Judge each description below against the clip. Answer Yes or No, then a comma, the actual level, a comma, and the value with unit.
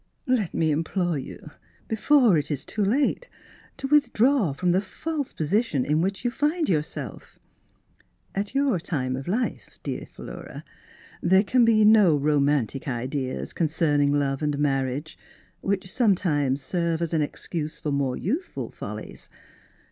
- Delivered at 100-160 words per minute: Yes, average, 150 wpm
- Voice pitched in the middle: Yes, medium, 170 Hz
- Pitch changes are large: Yes, wide, 7.1 semitones